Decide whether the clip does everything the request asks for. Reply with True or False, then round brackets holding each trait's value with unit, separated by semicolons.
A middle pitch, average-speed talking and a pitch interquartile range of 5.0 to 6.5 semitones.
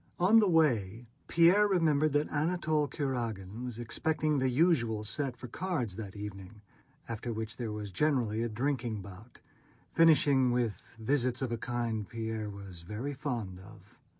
False (120 Hz; 150 wpm; 5.4 semitones)